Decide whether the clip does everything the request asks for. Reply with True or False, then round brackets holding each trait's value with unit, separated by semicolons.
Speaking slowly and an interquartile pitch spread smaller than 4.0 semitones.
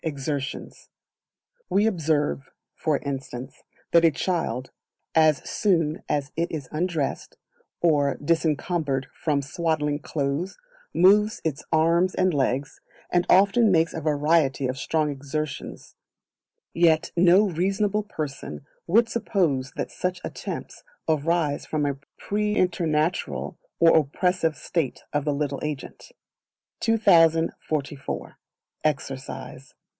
True (110 wpm; 3.5 semitones)